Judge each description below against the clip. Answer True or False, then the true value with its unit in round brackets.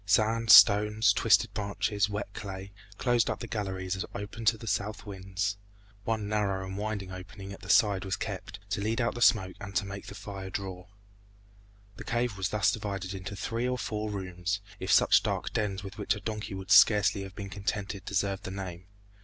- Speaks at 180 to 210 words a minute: True (195 wpm)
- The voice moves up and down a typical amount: False (1.9 semitones)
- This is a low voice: True (100 Hz)